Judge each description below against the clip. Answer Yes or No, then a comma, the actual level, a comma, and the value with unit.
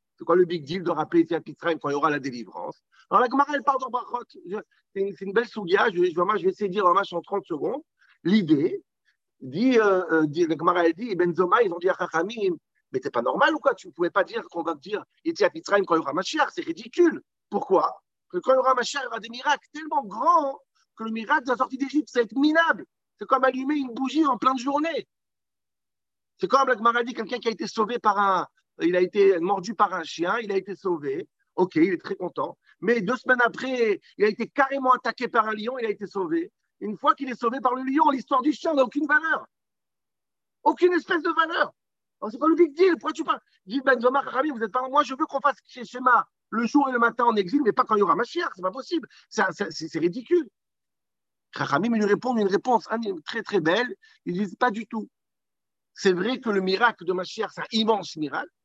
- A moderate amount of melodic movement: No, wide, 6.5 semitones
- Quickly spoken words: Yes, fast, 245 wpm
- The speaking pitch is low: No, high, 235 Hz